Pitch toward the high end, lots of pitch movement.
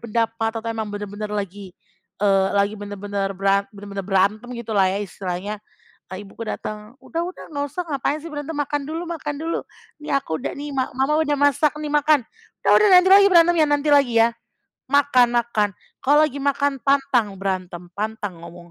Yes: high, 230 Hz; wide, 6.3 semitones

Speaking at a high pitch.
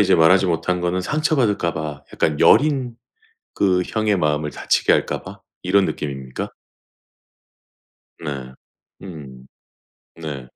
No: very low, 85 Hz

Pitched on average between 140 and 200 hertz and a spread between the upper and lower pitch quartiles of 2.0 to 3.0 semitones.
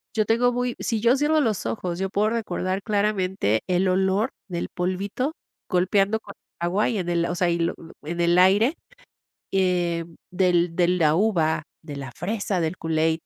No: medium, 185 Hz; average, 3.6 semitones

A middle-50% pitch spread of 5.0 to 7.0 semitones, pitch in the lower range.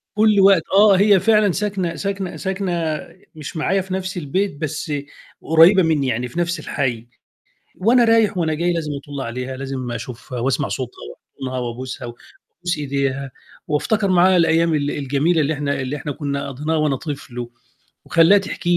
No: wide, 5.4 semitones; medium, 155 Hz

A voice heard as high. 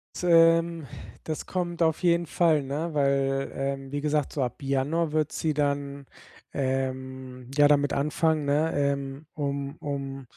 No: medium, 145 Hz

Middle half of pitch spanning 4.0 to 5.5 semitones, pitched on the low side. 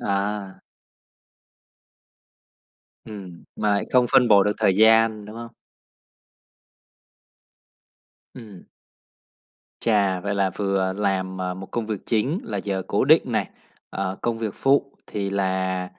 No: average, 2.8 semitones; low, 100 Hz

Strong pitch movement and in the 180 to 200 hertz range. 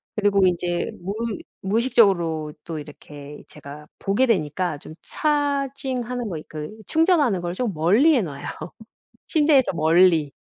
Yes: wide, 8.1 semitones; high, 190 Hz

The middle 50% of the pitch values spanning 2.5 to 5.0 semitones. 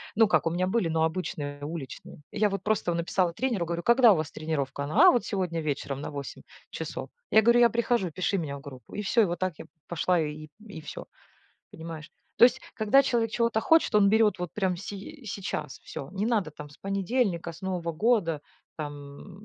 No: wide, 5.6 semitones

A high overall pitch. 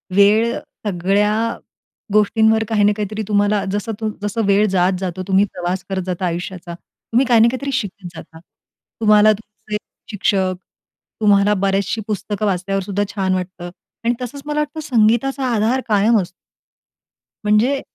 Yes: high, 205 Hz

